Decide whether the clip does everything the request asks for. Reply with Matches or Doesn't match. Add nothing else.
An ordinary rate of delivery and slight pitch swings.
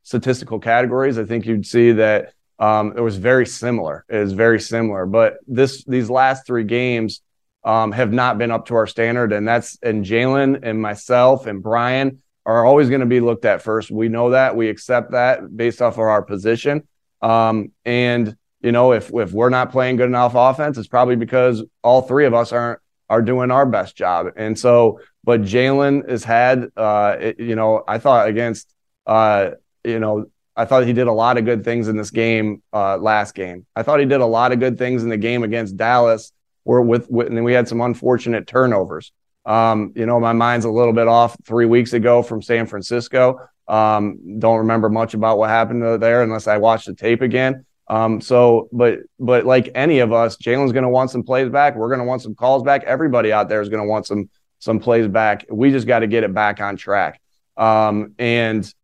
Doesn't match